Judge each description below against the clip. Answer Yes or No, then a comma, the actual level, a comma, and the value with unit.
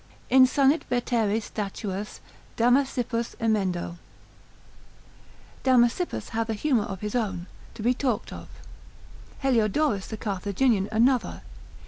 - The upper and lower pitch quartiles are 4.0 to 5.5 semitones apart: No, average, 3.6 semitones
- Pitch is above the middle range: Yes, high, 225 Hz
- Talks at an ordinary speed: No, slow, 100 wpm